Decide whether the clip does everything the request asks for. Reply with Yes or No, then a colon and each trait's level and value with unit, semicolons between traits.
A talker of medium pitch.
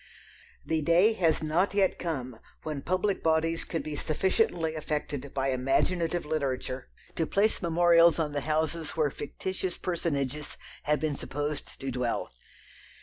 Yes: medium, 155 Hz